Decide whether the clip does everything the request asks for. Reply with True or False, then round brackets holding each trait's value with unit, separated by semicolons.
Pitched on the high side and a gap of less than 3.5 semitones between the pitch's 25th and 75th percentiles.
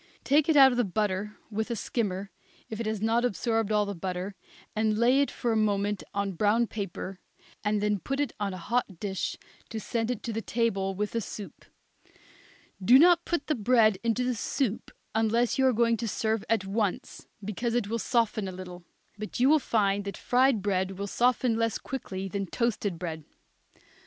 True (215 Hz; 3.1 semitones)